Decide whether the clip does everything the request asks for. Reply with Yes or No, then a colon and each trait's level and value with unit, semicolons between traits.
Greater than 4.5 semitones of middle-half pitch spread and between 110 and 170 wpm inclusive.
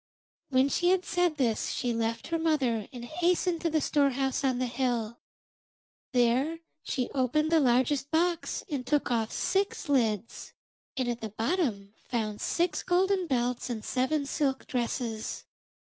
Yes: average, 5.0 semitones; average, 150 wpm